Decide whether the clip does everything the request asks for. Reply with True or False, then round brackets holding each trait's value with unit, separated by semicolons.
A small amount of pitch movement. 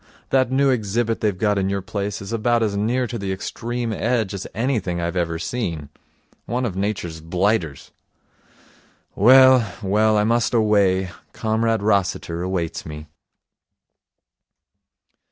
False (3.8 semitones)